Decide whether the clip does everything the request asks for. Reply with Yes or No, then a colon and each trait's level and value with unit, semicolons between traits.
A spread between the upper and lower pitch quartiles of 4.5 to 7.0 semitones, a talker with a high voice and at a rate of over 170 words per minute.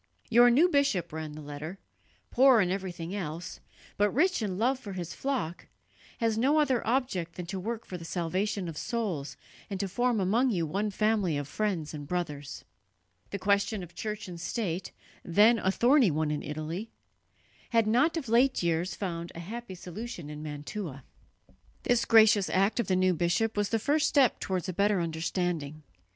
Yes: average, 5.3 semitones; high, 195 Hz; average, 180 wpm